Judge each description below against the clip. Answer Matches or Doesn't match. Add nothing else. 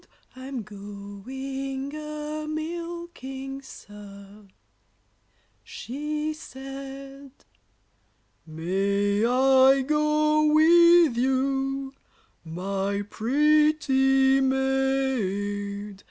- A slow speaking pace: Matches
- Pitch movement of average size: Doesn't match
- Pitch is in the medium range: Doesn't match